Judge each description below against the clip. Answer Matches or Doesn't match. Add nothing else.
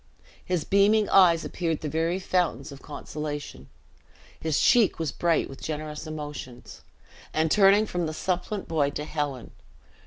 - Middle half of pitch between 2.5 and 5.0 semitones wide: Matches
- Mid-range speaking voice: Matches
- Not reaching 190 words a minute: Matches